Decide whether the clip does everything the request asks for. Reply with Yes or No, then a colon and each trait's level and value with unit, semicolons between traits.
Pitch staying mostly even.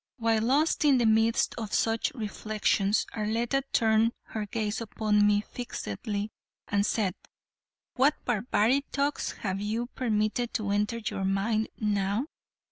Yes: narrow, 2.1 semitones